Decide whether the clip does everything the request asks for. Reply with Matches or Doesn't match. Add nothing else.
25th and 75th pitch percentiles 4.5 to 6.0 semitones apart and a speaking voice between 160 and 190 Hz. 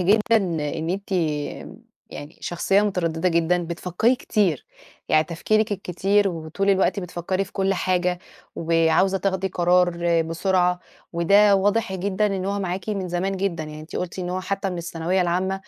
Doesn't match